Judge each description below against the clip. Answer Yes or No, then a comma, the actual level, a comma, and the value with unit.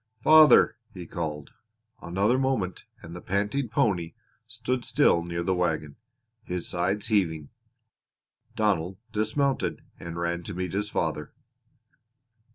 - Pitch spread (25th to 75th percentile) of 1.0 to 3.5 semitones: No, average, 4.3 semitones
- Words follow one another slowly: Yes, slow, 120 wpm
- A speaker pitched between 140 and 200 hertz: No, very low, 95 Hz